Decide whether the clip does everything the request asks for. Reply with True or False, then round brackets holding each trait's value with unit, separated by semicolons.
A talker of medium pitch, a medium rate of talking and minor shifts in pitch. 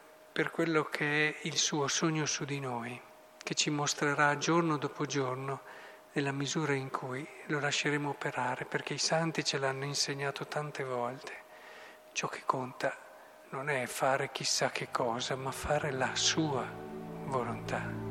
True (145 Hz; 150 wpm; 2.2 semitones)